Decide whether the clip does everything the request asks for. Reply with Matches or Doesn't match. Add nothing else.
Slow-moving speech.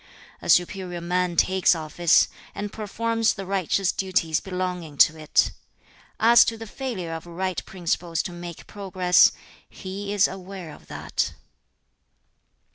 Matches